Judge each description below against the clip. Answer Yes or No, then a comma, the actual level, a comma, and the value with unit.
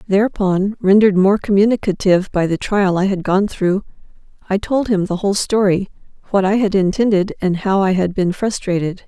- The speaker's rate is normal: Yes, average, 180 wpm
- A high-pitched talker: Yes, high, 195 Hz